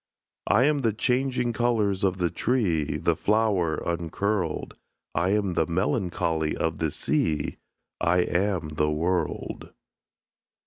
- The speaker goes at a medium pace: No, slow, 125 wpm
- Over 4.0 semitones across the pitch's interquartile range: Yes, average, 4.7 semitones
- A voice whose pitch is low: Yes, very low, 90 Hz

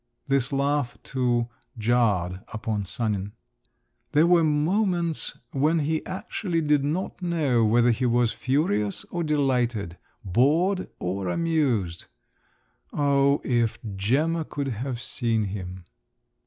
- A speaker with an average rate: No, slow, 115 wpm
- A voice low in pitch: Yes, low, 130 Hz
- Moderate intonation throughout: No, wide, 5.8 semitones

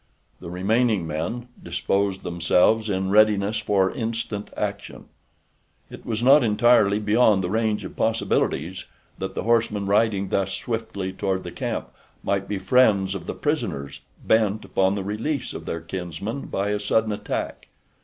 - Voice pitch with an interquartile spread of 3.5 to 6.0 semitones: No, average, 2.8 semitones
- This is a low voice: Yes, low, 105 Hz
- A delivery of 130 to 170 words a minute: Yes, average, 150 wpm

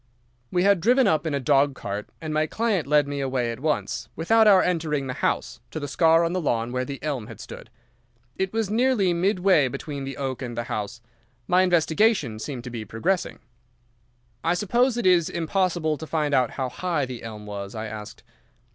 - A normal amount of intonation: No, wide, 6.2 semitones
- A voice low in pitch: No, medium, 155 Hz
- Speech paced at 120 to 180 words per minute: No, average, 200 wpm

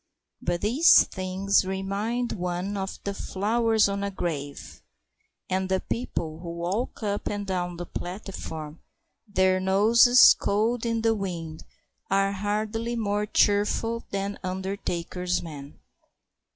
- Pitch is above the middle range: Yes, high, 195 Hz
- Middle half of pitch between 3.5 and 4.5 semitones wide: No, average, 2.8 semitones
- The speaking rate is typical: No, slow, 125 wpm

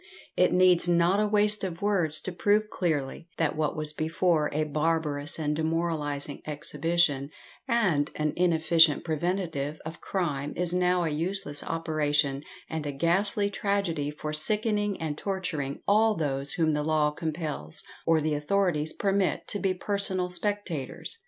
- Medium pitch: Yes, medium, 165 Hz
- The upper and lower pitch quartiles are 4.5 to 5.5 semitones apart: No, average, 3.9 semitones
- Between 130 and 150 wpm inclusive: Yes, average, 145 wpm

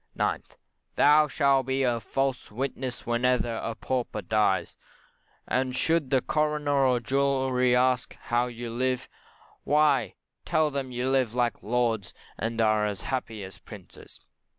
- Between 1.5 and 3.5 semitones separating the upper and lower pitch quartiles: Yes, narrow, 2.5 semitones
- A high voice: No, low, 125 Hz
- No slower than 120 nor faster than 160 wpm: Yes, average, 145 wpm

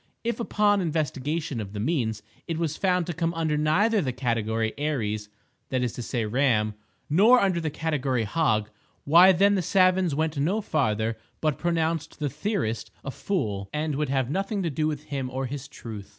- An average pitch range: No, wide, 5.8 semitones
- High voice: No, medium, 150 Hz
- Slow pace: No, average, 185 wpm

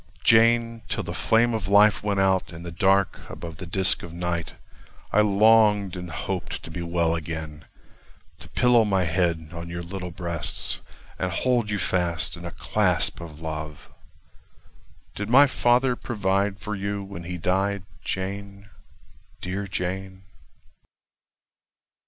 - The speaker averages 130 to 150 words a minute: Yes, average, 145 wpm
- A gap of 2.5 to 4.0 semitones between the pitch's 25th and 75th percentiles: Yes, average, 3.3 semitones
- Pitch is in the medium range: No, very low, 95 Hz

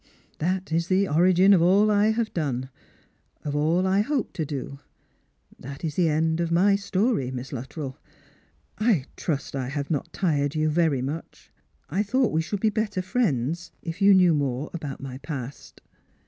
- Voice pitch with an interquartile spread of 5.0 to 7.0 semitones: Yes, average, 5.3 semitones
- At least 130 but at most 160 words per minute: No, average, 175 wpm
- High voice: No, medium, 165 Hz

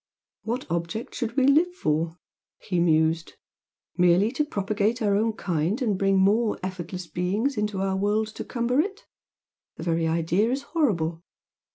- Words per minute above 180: No, average, 155 wpm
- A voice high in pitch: Yes, high, 200 Hz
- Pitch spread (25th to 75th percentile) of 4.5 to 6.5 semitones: Yes, wide, 5.4 semitones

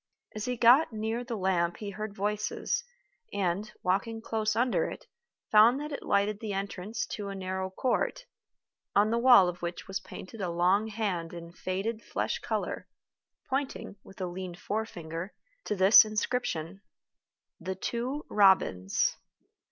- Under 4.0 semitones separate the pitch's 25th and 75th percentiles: Yes, average, 3.2 semitones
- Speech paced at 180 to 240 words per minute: No, average, 150 wpm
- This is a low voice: No, high, 205 Hz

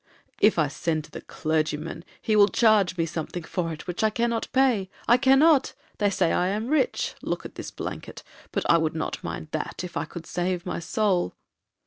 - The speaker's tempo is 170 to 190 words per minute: Yes, average, 185 wpm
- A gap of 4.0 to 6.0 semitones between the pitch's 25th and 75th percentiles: Yes, average, 5.0 semitones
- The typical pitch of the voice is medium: Yes, medium, 180 Hz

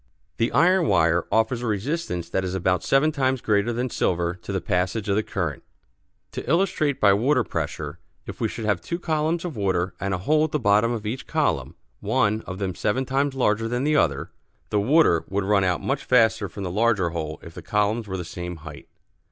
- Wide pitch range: Yes, wide, 6.1 semitones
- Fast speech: Yes, fast, 215 wpm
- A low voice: Yes, low, 105 Hz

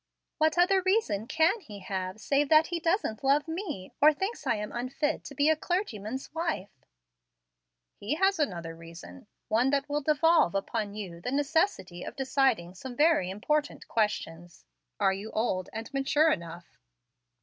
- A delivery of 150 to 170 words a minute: Yes, average, 160 wpm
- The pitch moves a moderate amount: No, wide, 8.1 semitones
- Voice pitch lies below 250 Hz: No, very high, 270 Hz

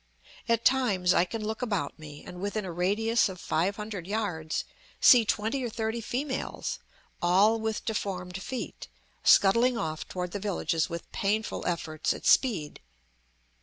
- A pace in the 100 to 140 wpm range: No, average, 150 wpm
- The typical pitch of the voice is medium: No, high, 205 Hz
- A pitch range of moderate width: Yes, average, 3.9 semitones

